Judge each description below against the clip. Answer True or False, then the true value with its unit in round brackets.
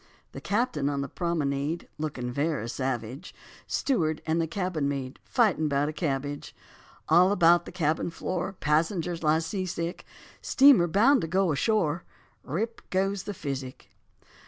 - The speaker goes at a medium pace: True (145 wpm)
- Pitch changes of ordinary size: True (4.5 semitones)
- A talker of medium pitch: True (165 Hz)